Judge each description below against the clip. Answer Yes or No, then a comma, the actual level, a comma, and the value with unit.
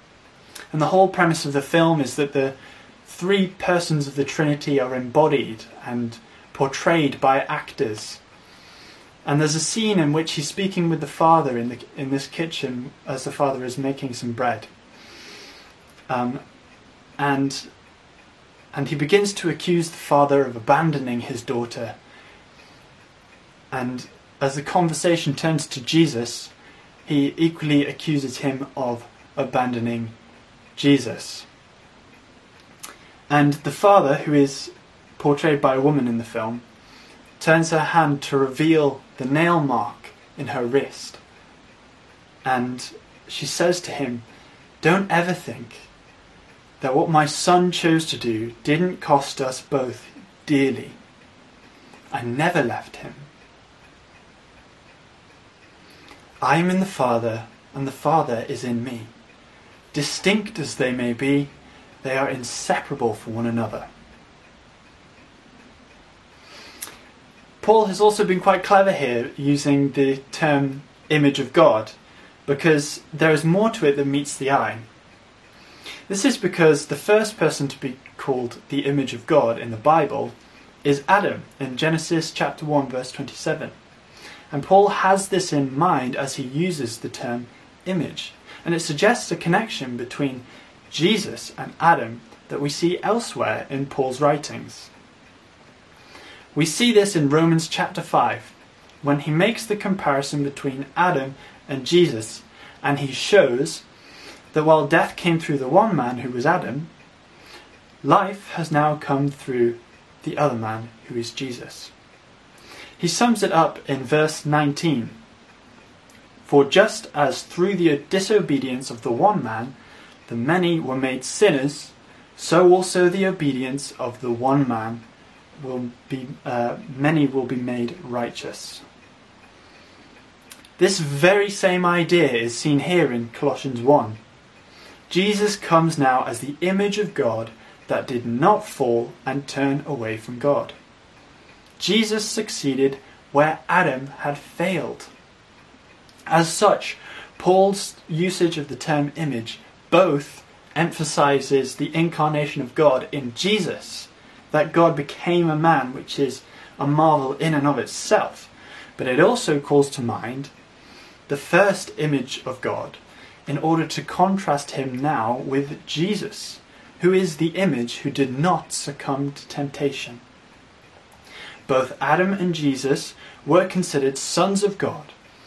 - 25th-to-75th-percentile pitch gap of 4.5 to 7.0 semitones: No, average, 4.1 semitones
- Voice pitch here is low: No, medium, 145 Hz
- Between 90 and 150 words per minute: Yes, slow, 135 wpm